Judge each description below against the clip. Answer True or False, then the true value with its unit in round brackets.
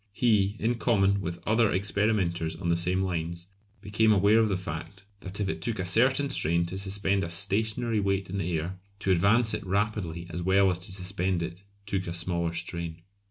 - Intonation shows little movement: False (3.3 semitones)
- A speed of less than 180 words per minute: False (200 wpm)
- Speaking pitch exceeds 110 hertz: False (95 Hz)